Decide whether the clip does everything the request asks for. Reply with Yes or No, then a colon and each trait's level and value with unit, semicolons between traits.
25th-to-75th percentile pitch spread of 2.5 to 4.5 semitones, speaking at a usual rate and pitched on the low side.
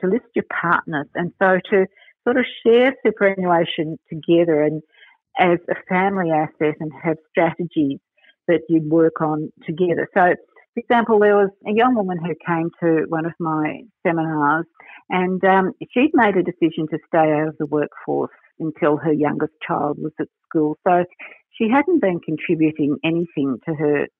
No: average, 3.9 semitones; average, 165 wpm; medium, 170 Hz